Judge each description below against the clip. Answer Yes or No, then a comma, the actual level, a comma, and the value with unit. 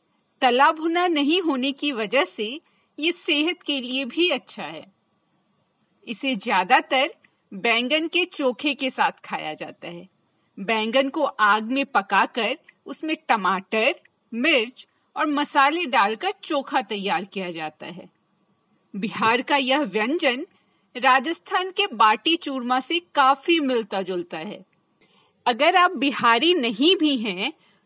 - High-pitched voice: Yes, very high, 275 Hz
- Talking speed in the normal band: Yes, average, 125 wpm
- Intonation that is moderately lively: No, wide, 6.0 semitones